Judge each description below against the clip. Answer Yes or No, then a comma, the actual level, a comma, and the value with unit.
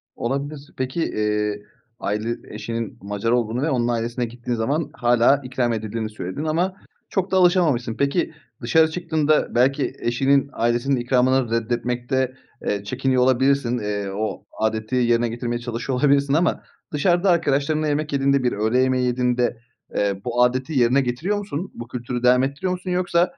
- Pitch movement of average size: Yes, average, 3.3 semitones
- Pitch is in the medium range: No, low, 125 Hz